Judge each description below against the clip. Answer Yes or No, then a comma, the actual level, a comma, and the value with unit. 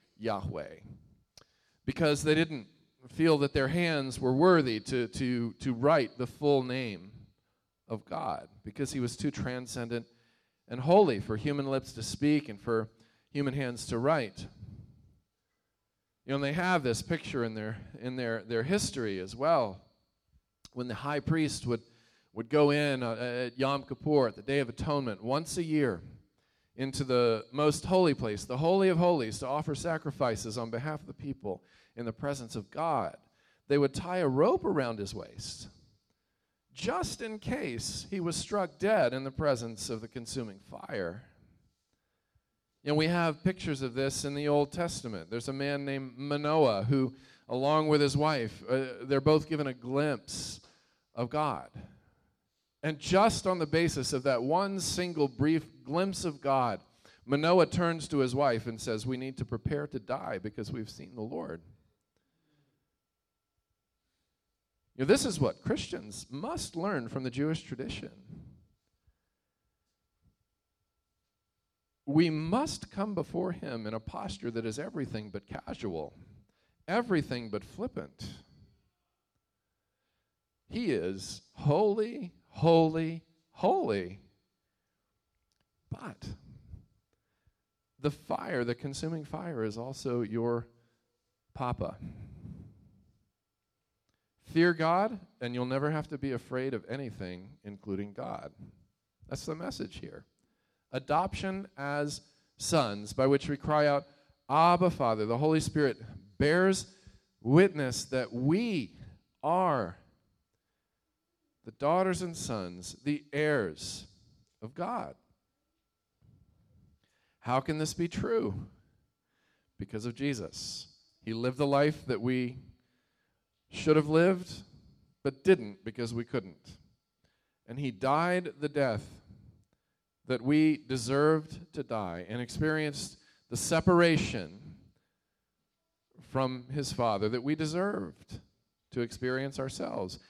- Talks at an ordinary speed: No, slow, 130 wpm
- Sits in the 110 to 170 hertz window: Yes, low, 135 Hz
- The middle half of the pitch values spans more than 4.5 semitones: Yes, average, 5.2 semitones